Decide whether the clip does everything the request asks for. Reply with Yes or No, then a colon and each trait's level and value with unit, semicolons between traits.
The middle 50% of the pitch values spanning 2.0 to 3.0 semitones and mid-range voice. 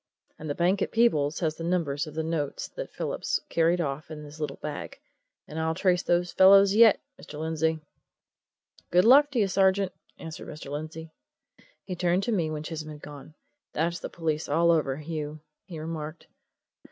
Yes: average, 2.7 semitones; medium, 160 Hz